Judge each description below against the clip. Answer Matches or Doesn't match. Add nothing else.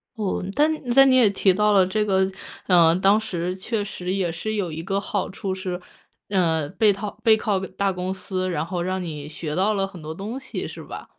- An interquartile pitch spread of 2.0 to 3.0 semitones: Matches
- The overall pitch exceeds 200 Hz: Doesn't match